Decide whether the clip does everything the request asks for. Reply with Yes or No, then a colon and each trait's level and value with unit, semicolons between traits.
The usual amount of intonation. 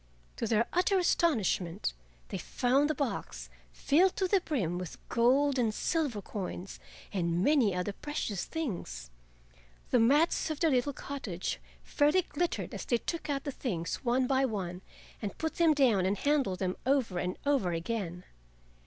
No: wide, 7.7 semitones